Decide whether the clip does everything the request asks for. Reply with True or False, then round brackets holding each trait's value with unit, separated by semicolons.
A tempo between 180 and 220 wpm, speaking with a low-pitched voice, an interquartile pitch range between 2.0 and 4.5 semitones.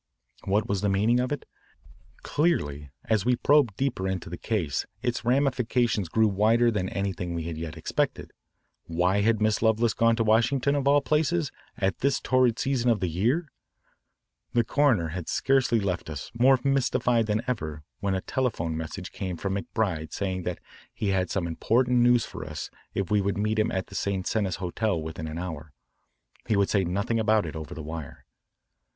False (185 wpm; 105 Hz; 5.1 semitones)